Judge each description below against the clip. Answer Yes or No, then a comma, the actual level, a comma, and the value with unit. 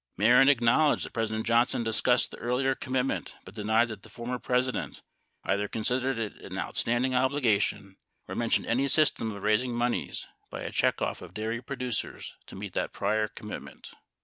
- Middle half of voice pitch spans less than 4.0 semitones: Yes, average, 2.7 semitones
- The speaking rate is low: No, average, 175 wpm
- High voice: No, low, 120 Hz